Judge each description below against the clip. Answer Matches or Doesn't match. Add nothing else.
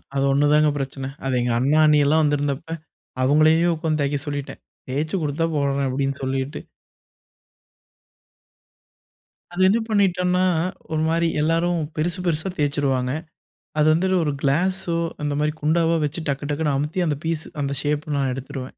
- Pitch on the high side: Doesn't match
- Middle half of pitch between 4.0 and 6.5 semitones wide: Doesn't match